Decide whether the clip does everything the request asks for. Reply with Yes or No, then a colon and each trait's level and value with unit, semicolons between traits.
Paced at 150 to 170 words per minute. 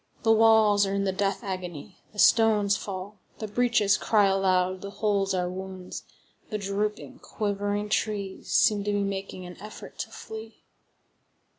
Yes: average, 155 wpm